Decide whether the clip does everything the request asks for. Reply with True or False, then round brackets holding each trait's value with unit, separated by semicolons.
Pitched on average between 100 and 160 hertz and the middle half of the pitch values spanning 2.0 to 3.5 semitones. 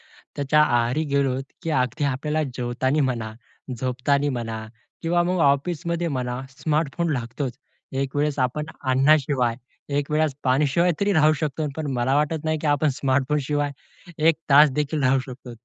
True (140 Hz; 3.0 semitones)